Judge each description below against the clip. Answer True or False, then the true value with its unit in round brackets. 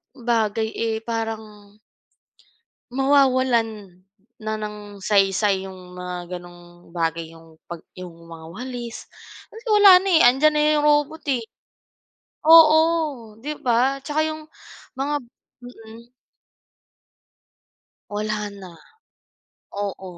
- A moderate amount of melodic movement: False (6.3 semitones)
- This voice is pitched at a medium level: False (220 Hz)